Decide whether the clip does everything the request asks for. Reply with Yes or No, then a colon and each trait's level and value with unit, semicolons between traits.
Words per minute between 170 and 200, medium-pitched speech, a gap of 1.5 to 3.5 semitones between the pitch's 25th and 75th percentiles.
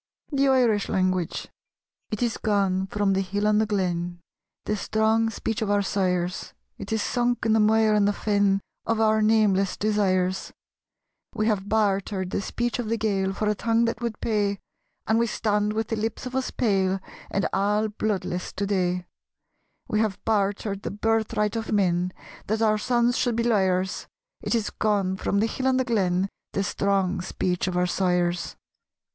No: average, 180 wpm; high, 210 Hz; narrow, 2.5 semitones